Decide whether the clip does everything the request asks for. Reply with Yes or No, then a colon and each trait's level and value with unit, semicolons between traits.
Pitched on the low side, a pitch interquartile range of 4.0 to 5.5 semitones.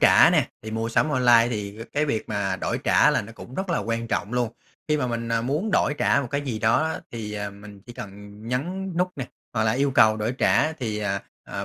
Yes: low, 115 Hz; average, 4.4 semitones